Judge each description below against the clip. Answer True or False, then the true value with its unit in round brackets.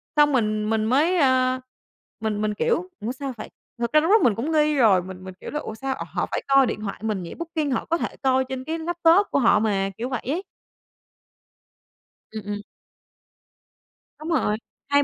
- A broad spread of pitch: True (5.8 semitones)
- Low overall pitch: False (260 Hz)